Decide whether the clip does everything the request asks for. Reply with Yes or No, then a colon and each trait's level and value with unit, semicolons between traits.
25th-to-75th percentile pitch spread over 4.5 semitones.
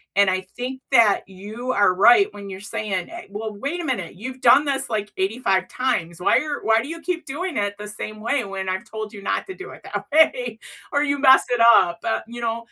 Yes: average, 5.0 semitones